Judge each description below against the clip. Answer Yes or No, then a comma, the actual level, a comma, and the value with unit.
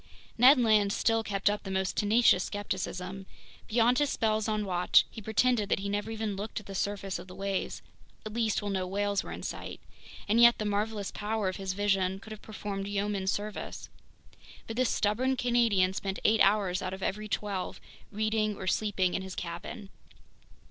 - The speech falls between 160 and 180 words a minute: No, average, 190 wpm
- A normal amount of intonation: No, narrow, 2.1 semitones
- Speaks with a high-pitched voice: Yes, high, 205 Hz